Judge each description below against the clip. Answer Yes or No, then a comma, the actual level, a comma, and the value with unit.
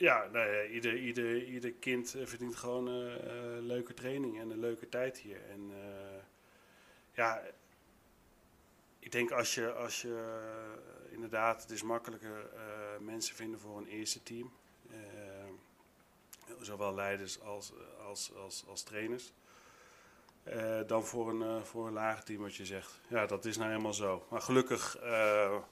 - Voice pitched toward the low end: Yes, low, 110 Hz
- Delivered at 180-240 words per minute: No, average, 155 wpm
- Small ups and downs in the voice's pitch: Yes, narrow, 2.3 semitones